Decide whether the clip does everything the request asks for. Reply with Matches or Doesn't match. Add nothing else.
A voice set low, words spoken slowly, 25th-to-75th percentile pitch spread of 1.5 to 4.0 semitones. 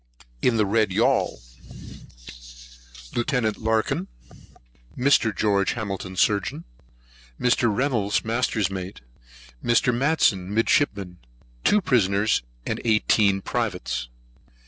Matches